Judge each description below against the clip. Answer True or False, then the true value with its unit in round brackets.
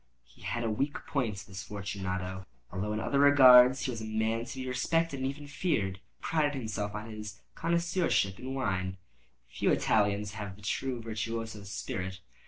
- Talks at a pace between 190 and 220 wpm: False (165 wpm)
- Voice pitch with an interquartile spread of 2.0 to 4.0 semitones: False (4.8 semitones)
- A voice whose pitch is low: True (110 Hz)